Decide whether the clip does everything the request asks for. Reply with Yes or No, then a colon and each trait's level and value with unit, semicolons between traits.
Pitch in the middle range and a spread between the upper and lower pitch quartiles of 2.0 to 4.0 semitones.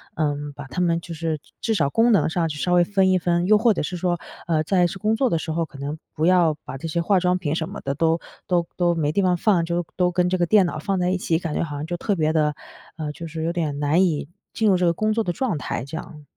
Yes: medium, 170 Hz; average, 2.8 semitones